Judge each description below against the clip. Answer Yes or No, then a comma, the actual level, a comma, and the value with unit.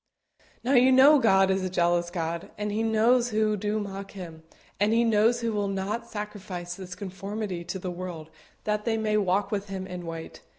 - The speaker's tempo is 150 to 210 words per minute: Yes, average, 200 wpm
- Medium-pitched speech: No, high, 200 Hz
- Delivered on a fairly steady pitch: No, average, 3.1 semitones